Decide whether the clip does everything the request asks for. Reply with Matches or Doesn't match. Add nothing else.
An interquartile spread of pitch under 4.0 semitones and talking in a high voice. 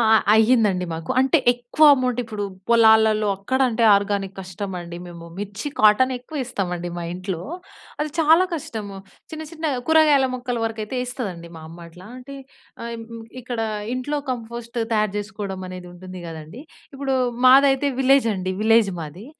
Doesn't match